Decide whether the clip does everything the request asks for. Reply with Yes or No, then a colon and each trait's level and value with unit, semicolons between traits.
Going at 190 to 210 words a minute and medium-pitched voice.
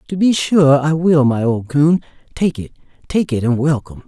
Yes: fast, 205 wpm; medium, 150 Hz